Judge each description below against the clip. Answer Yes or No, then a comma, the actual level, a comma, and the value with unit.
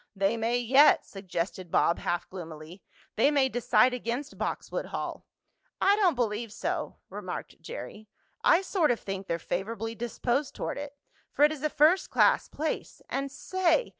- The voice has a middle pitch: No, high, 240 Hz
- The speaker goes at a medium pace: Yes, average, 160 wpm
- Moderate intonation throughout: No, wide, 6.8 semitones